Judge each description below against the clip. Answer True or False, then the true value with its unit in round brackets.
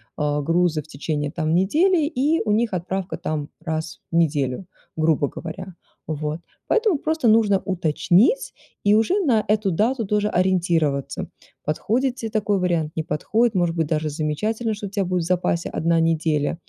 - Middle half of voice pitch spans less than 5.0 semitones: False (5.4 semitones)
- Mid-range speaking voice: True (180 Hz)